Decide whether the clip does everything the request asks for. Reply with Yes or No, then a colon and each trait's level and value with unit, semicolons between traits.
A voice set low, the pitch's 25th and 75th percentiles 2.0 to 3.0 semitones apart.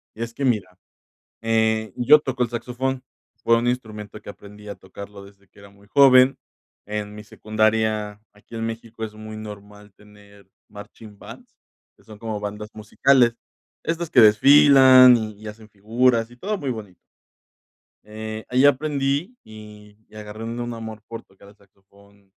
Yes: low, 110 Hz; average, 2.7 semitones